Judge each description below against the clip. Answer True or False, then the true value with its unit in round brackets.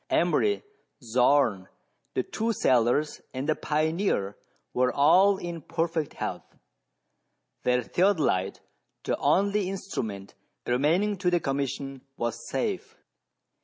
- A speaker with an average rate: False (105 wpm)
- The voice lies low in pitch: False (150 Hz)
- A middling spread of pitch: False (6.7 semitones)